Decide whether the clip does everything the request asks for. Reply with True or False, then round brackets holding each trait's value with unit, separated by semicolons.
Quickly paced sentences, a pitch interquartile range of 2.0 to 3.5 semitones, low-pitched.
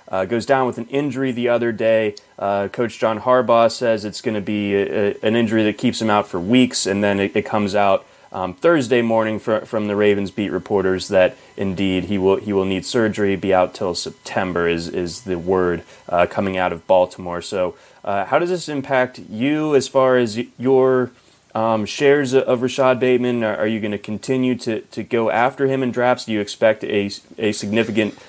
False (210 wpm; 4.0 semitones; 110 Hz)